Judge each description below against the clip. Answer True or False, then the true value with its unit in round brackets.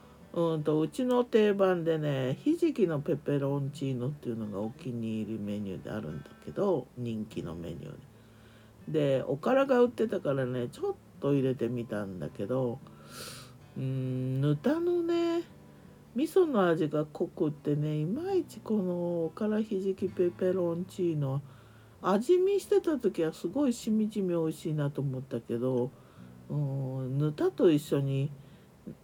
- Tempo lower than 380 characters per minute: True (290 characters per minute)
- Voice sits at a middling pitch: True (150 Hz)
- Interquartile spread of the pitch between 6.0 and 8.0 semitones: True (7.2 semitones)